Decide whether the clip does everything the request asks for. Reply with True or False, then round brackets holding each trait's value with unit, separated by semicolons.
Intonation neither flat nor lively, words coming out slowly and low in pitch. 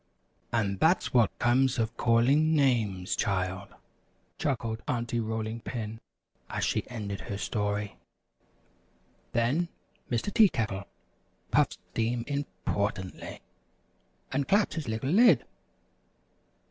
True (4.5 semitones; 105 wpm; 115 Hz)